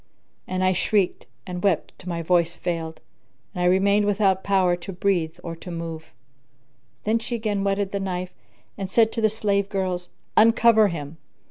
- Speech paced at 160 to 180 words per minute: Yes, average, 170 wpm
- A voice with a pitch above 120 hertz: Yes, high, 190 Hz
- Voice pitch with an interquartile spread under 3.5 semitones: Yes, narrow, 2.5 semitones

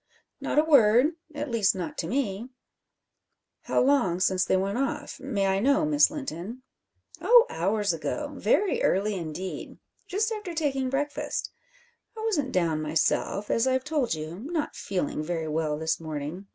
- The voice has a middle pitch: No, high, 220 Hz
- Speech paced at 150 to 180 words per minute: Yes, average, 155 wpm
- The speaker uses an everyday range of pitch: No, wide, 8.5 semitones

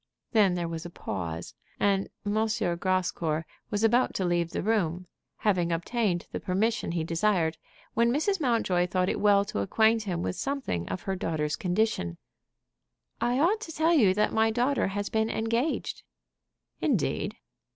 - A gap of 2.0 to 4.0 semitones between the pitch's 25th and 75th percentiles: No, average, 4.7 semitones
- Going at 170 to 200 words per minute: No, average, 160 wpm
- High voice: Yes, high, 200 Hz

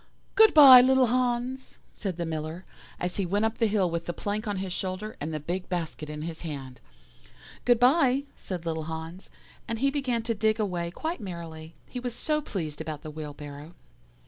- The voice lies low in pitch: No, medium, 185 Hz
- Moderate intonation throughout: No, wide, 7.0 semitones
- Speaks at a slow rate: No, average, 195 wpm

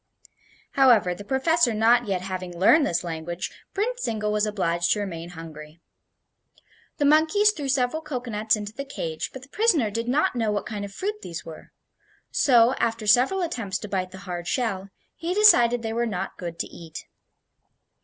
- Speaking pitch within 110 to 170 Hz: No, high, 220 Hz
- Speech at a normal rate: Yes, average, 175 wpm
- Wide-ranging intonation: Yes, wide, 6.5 semitones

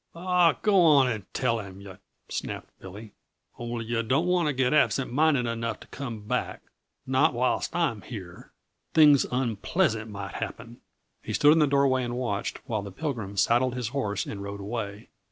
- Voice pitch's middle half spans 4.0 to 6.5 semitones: Yes, average, 5.1 semitones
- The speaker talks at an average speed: Yes, average, 180 wpm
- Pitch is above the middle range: No, low, 120 Hz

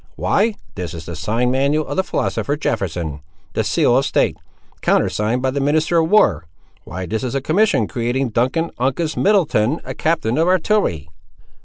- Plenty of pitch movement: Yes, wide, 7.1 semitones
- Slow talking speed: No, average, 170 wpm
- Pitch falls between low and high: No, low, 130 Hz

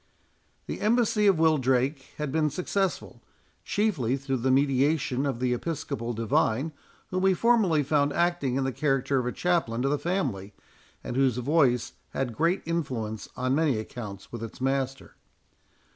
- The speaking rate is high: No, average, 155 wpm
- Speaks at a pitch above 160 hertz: No, low, 135 Hz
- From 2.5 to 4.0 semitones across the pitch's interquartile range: No, average, 4.7 semitones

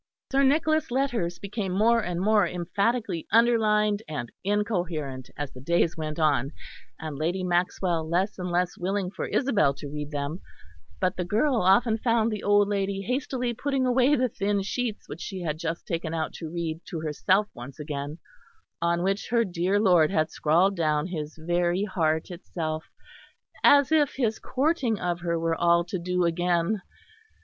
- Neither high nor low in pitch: Yes, medium, 180 Hz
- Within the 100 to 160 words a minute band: No, average, 170 wpm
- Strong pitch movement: No, average, 4.7 semitones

